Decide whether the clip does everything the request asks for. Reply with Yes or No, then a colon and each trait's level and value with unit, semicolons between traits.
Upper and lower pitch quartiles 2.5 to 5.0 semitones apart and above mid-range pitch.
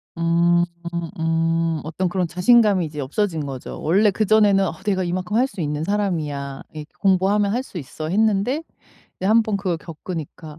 No: average, 3.8 semitones; medium, 175 Hz